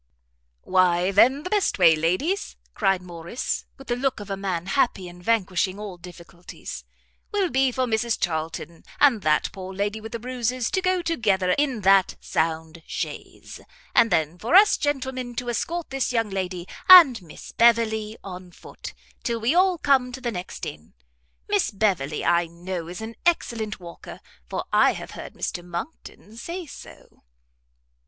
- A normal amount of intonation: No, wide, 6.3 semitones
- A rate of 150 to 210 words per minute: Yes, average, 165 wpm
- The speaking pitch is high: Yes, high, 215 Hz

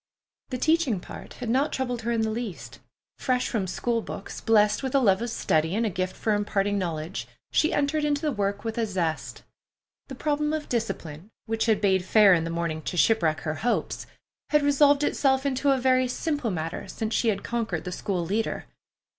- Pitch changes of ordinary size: No, wide, 5.8 semitones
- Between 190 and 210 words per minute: Yes, average, 200 wpm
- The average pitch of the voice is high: Yes, high, 225 Hz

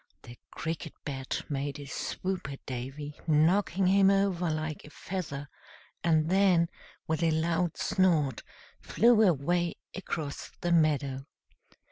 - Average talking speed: No, slow, 125 wpm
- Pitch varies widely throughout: No, average, 3.9 semitones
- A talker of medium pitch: Yes, medium, 160 Hz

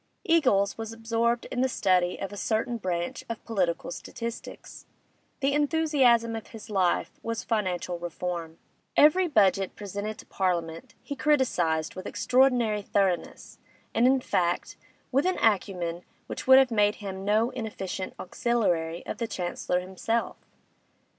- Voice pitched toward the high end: Yes, high, 210 Hz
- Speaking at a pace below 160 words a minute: Yes, average, 140 wpm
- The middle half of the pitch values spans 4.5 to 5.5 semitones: Yes, average, 4.9 semitones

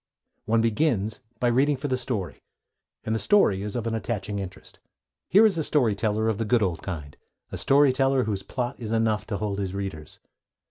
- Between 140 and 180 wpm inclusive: No, average, 200 wpm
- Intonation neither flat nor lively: Yes, average, 4.3 semitones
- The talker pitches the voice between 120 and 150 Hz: No, low, 110 Hz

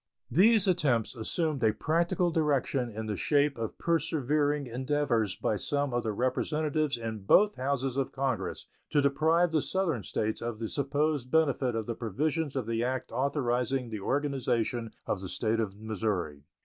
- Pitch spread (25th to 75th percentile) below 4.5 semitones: No, average, 4.9 semitones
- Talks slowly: No, average, 160 wpm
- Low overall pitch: Yes, low, 130 Hz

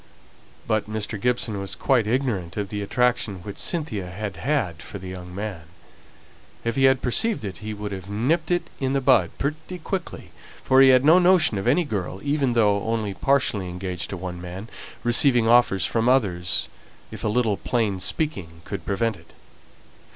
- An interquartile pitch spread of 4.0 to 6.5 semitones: Yes, wide, 5.4 semitones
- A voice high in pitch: No, low, 110 Hz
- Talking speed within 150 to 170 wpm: No, average, 180 wpm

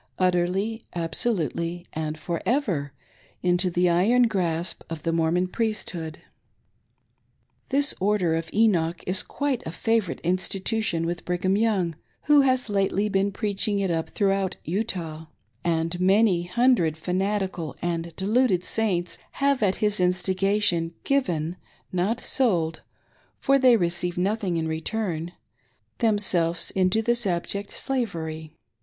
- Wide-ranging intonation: No, average, 4.1 semitones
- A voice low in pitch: No, medium, 185 Hz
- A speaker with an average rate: No, slow, 130 wpm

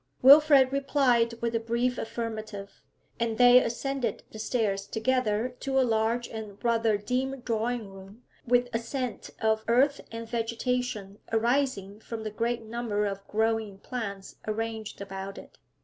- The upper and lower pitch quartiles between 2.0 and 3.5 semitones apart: Yes, narrow, 2.5 semitones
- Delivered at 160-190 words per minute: No, average, 145 wpm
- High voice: Yes, high, 230 Hz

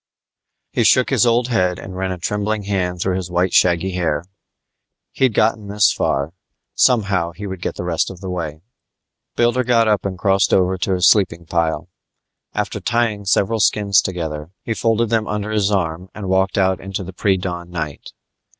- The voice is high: No, very low, 95 Hz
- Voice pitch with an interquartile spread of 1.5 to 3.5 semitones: Yes, average, 3.1 semitones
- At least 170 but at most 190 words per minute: Yes, average, 185 wpm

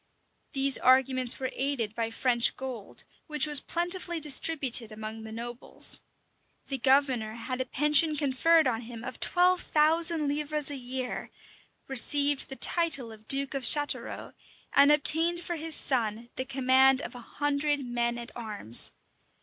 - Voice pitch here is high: Yes, very high, 270 Hz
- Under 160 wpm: Yes, average, 150 wpm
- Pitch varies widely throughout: No, average, 3.8 semitones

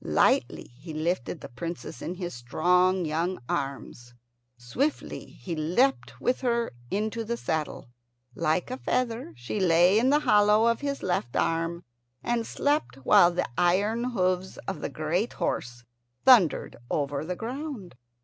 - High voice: No, medium, 180 Hz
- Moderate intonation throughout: No, wide, 6.6 semitones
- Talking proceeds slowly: No, average, 145 wpm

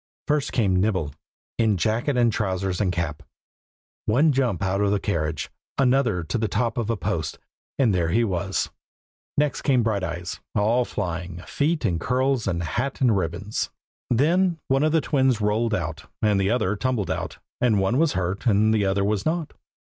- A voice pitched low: Yes, low, 105 Hz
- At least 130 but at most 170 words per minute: No, average, 180 wpm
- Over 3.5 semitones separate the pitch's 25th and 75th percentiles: Yes, average, 5.2 semitones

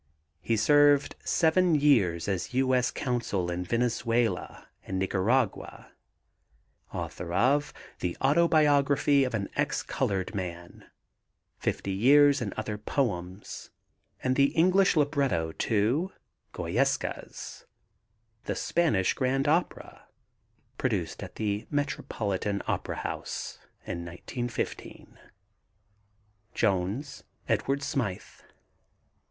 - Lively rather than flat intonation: Yes, wide, 6.8 semitones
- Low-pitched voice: Yes, low, 120 Hz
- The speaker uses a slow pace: Yes, slow, 95 wpm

